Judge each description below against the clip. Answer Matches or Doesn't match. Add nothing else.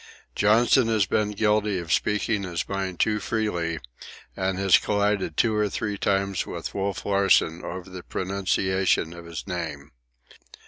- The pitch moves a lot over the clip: Doesn't match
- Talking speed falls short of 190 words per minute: Matches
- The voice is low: Matches